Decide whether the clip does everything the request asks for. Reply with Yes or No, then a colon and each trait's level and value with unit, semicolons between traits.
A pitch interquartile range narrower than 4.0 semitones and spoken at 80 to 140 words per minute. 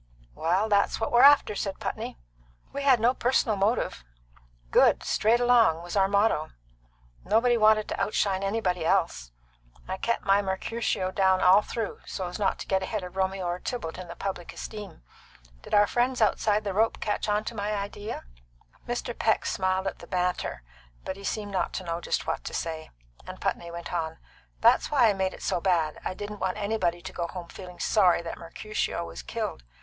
No: average, 3.1 semitones; average, 195 wpm